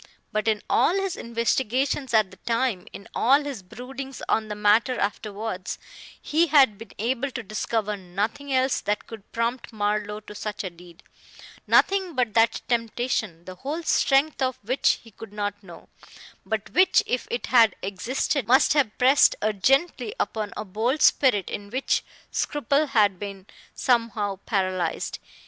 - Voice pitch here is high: Yes, high, 225 Hz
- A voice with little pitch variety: No, average, 4.3 semitones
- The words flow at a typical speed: Yes, average, 155 wpm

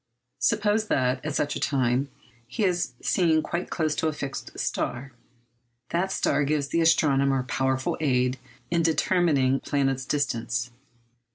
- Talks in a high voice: No, medium, 140 Hz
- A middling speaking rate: Yes, average, 145 wpm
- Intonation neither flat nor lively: Yes, average, 3.7 semitones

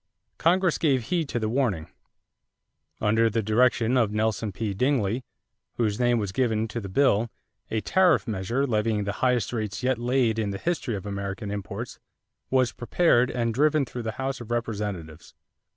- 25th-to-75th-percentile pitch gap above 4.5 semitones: No, average, 3.3 semitones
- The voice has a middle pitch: No, low, 115 Hz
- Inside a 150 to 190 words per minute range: Yes, average, 170 wpm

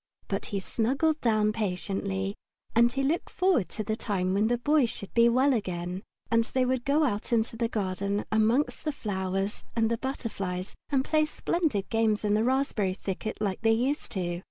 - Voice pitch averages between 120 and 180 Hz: No, high, 220 Hz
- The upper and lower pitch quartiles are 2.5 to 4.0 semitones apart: No, average, 4.6 semitones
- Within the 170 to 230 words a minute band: Yes, average, 180 wpm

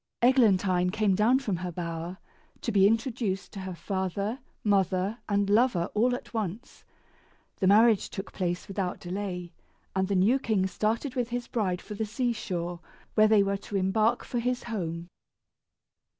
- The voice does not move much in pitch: No, average, 3.6 semitones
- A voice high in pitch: Yes, high, 200 Hz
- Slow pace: No, average, 165 wpm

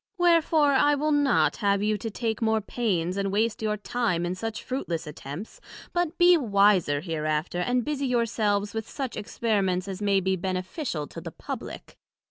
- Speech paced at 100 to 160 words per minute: No, average, 175 wpm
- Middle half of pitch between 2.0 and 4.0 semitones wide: No, average, 5.2 semitones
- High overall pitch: Yes, high, 210 Hz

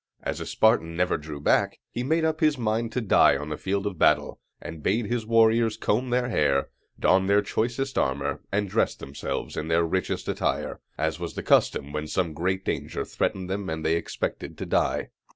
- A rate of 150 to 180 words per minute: No, average, 200 wpm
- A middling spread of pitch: No, wide, 6.1 semitones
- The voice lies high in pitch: No, very low, 95 Hz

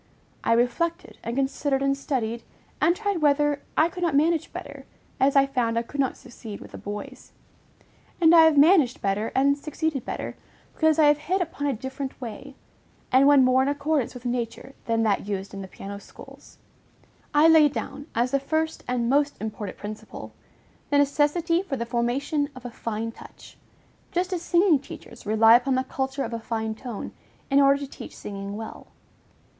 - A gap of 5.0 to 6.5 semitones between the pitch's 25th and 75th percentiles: No, average, 4.2 semitones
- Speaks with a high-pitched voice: Yes, very high, 270 Hz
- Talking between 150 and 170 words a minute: No, average, 185 wpm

